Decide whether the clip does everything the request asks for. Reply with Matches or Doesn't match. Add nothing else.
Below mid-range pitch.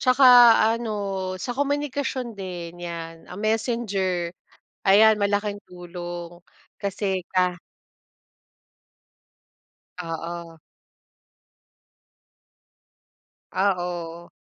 Doesn't match